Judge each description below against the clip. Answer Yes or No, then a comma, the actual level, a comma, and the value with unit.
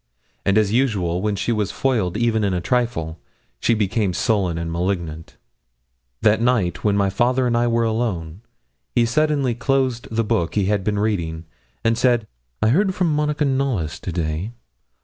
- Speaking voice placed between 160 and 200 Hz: No, low, 110 Hz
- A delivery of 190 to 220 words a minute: No, average, 170 wpm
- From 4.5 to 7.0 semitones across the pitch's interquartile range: Yes, average, 4.9 semitones